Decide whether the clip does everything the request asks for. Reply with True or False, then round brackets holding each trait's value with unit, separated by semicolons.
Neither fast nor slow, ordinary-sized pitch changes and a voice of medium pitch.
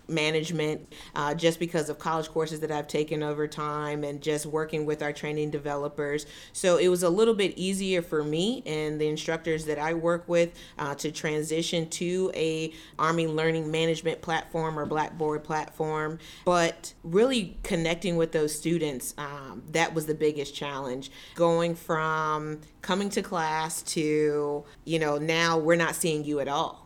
False (165 wpm; 1.7 semitones; 155 Hz)